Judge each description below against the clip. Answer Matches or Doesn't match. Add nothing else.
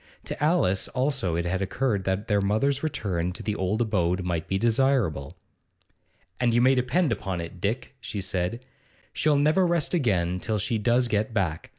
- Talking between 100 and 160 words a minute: Doesn't match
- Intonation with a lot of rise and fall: Matches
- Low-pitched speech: Matches